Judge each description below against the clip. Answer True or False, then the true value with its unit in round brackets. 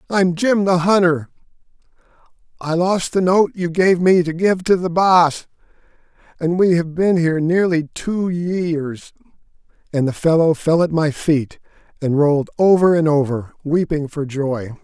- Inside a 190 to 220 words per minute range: False (160 wpm)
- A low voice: False (165 Hz)